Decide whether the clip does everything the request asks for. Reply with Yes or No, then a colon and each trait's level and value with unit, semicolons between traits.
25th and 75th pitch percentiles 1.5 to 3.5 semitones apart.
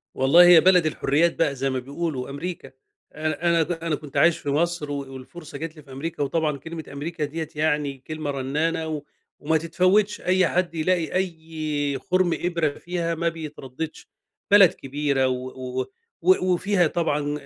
Yes: average, 3.0 semitones